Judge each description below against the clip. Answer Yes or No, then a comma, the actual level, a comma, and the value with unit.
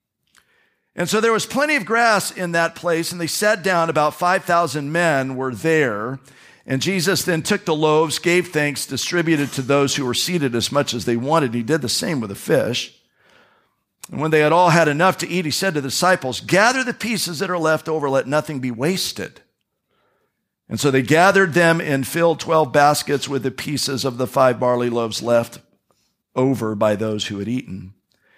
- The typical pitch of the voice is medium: Yes, medium, 155 Hz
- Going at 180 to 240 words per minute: Yes, average, 200 wpm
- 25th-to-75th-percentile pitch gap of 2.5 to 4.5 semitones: No, average, 5.0 semitones